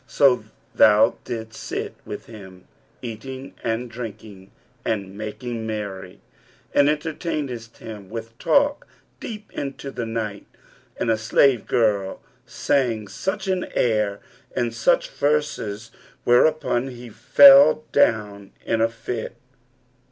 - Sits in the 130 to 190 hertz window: No, low, 115 Hz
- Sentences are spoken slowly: Yes, slow, 115 wpm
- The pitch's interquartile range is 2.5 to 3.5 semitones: No, average, 4.0 semitones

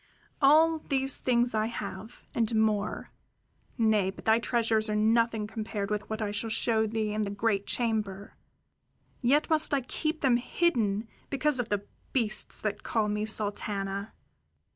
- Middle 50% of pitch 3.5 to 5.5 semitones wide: No, narrow, 2.5 semitones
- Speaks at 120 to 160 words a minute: Yes, average, 155 wpm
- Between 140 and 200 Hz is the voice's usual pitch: No, high, 220 Hz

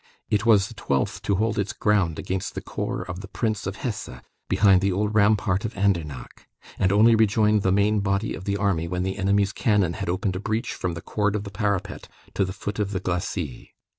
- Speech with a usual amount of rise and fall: No, narrow, 2.1 semitones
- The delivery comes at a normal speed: No, fast, 220 wpm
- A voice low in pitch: Yes, low, 100 Hz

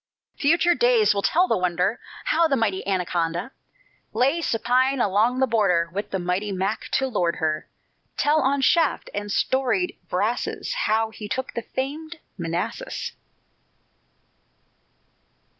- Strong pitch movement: Yes, wide, 6.3 semitones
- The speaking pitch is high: Yes, high, 225 Hz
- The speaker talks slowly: Yes, slow, 130 wpm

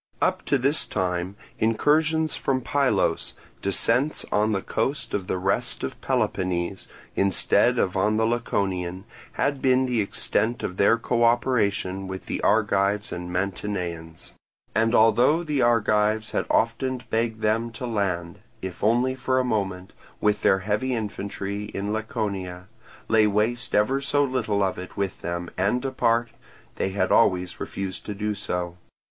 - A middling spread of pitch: Yes, average, 3.9 semitones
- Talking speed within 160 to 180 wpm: No, average, 150 wpm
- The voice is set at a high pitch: No, low, 105 Hz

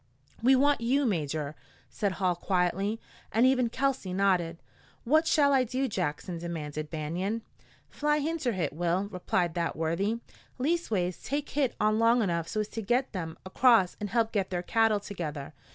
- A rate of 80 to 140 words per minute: No, average, 160 wpm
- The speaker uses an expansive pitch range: Yes, wide, 6.3 semitones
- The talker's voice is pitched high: Yes, high, 200 Hz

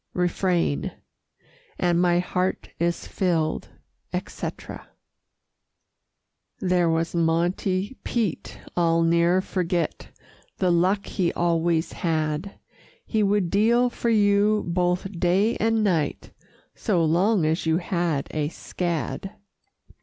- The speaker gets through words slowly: Yes, slow, 105 wpm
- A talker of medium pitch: Yes, medium, 175 Hz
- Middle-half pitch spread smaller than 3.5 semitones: Yes, average, 2.8 semitones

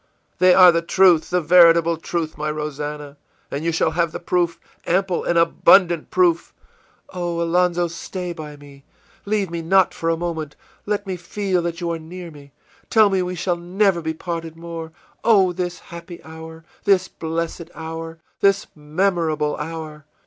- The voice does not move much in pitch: Yes, narrow, 2.0 semitones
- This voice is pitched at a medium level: Yes, medium, 170 Hz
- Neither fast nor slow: Yes, average, 170 wpm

